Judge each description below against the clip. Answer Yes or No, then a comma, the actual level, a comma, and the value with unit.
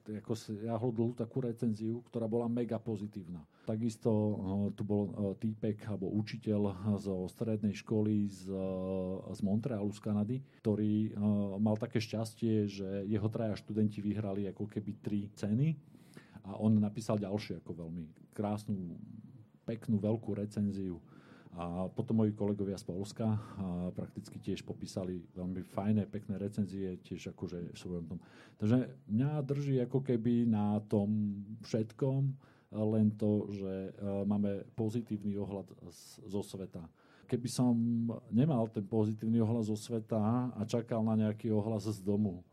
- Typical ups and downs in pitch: No, narrow, 2.3 semitones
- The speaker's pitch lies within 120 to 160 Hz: No, low, 105 Hz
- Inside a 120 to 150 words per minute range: Yes, average, 135 wpm